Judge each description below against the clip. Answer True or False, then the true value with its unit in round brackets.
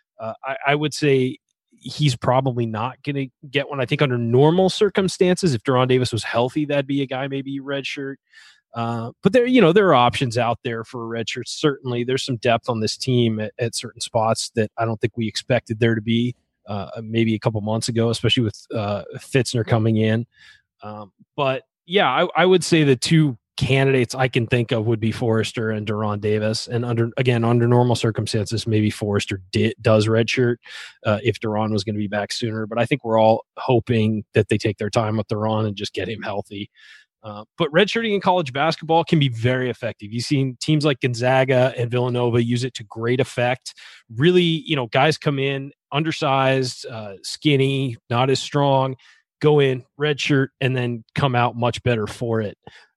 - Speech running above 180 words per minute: True (200 wpm)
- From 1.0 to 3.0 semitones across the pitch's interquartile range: False (3.4 semitones)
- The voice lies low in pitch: True (120 Hz)